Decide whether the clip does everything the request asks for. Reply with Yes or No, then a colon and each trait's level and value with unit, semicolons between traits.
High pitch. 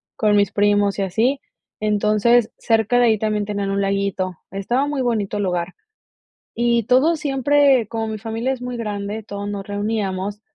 Yes: high, 215 Hz